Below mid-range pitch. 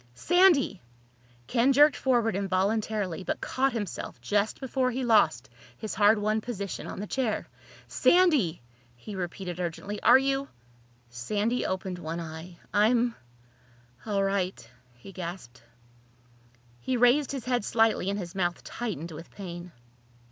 No: high, 200 Hz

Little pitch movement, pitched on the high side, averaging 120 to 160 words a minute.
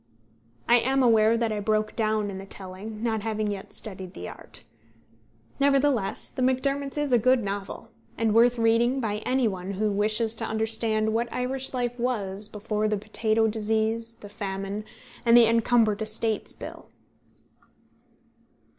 Yes: narrow, 2.2 semitones; high, 220 Hz; average, 155 wpm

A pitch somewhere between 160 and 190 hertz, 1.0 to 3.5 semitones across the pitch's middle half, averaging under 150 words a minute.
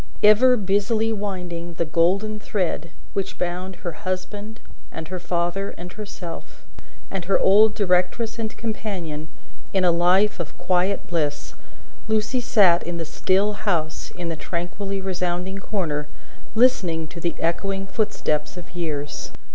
Yes: medium, 185 Hz; average, 3.2 semitones; average, 140 wpm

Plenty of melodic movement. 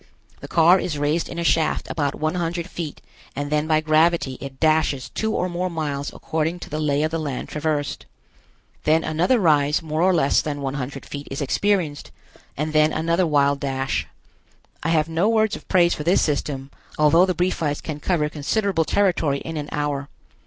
No: average, 2.8 semitones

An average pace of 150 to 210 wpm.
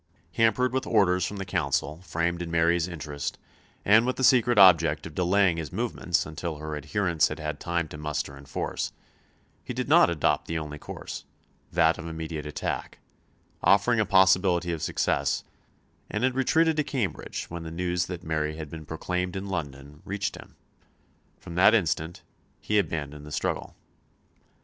Yes: average, 170 wpm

